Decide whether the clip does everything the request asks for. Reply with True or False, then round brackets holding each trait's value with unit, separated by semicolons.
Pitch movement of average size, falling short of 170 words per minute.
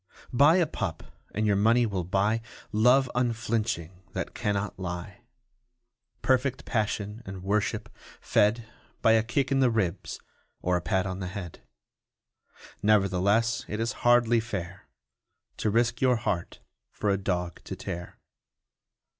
True (3.7 semitones; 140 wpm)